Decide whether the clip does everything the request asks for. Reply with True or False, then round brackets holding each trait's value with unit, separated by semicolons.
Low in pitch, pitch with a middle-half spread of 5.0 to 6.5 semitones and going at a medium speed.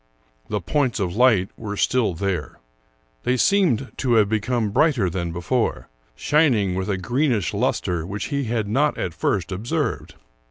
True (105 Hz; 5.4 semitones; 155 wpm)